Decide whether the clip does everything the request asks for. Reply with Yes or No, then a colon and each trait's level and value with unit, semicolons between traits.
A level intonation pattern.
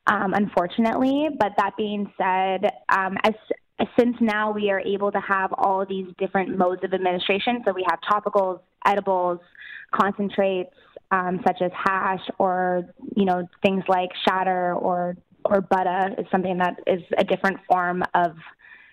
Yes: narrow, 1.8 semitones